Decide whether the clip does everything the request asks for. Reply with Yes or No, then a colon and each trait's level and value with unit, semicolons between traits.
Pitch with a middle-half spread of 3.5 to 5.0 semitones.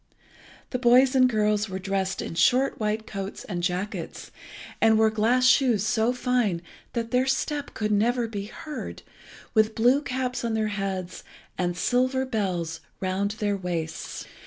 Yes: average, 4.3 semitones